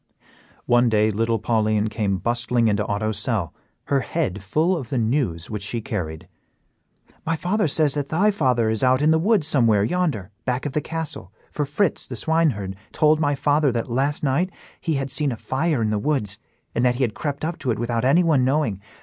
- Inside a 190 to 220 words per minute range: Yes, average, 200 wpm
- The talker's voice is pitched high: No, low, 130 Hz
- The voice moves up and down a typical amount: No, wide, 5.8 semitones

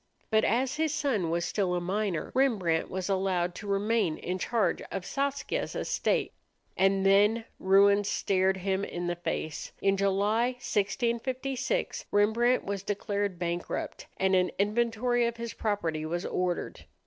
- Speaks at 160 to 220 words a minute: No, average, 145 wpm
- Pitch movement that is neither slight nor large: Yes, average, 4.0 semitones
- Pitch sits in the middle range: No, high, 200 Hz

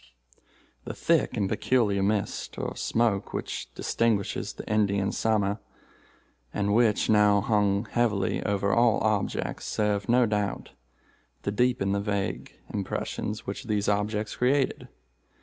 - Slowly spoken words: Yes, slow, 125 wpm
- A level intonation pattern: Yes, narrow, 1.9 semitones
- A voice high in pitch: No, low, 105 Hz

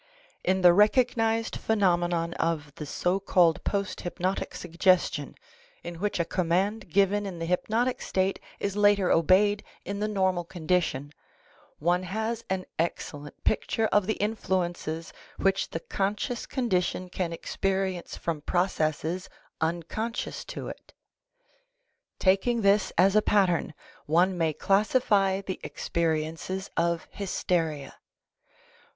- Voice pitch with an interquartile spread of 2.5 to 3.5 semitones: Yes, average, 3.1 semitones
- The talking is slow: Yes, slow, 120 wpm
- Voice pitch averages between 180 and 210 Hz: Yes, medium, 185 Hz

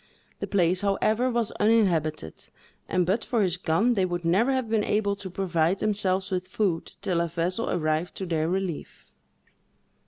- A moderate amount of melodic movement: Yes, average, 3.6 semitones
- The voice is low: No, medium, 185 Hz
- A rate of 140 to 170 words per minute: Yes, average, 165 wpm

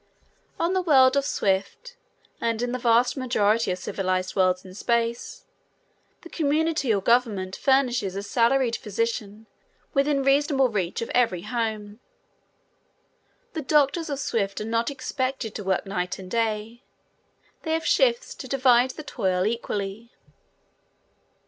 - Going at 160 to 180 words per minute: No, slow, 135 wpm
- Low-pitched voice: No, high, 235 Hz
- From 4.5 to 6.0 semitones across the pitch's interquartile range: Yes, average, 5.0 semitones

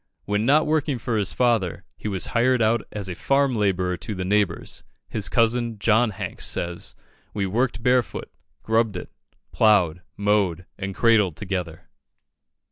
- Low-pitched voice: Yes, low, 105 Hz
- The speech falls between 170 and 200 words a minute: No, average, 150 wpm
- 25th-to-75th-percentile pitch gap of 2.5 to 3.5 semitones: No, average, 3.9 semitones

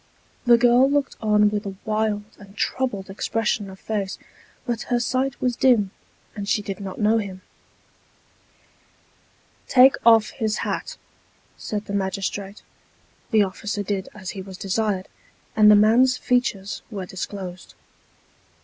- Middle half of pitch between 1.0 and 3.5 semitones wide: Yes, average, 2.8 semitones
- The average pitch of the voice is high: Yes, high, 210 Hz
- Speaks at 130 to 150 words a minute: Yes, average, 140 wpm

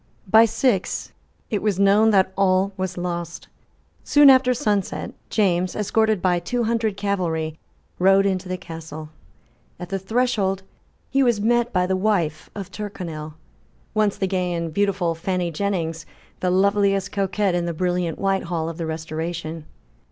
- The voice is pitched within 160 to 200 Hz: Yes, high, 190 Hz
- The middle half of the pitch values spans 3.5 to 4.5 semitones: No, average, 3.1 semitones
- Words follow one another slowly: No, average, 150 wpm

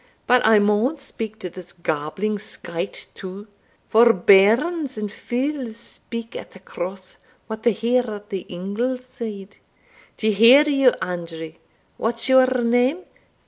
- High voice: Yes, high, 220 Hz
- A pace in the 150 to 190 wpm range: No, average, 140 wpm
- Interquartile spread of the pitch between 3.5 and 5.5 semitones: Yes, average, 4.4 semitones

